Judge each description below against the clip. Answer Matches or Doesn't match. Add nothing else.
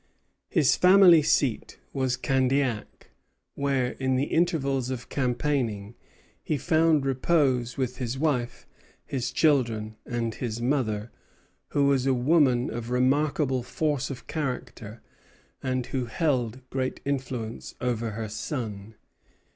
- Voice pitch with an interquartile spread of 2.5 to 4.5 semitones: Matches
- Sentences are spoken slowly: Matches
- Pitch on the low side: Matches